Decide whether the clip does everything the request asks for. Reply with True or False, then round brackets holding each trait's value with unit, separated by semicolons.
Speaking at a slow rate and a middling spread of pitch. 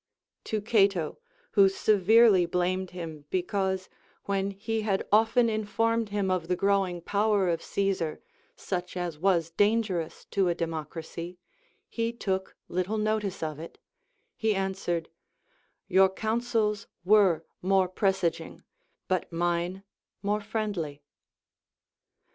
True (115 wpm; 3.2 semitones)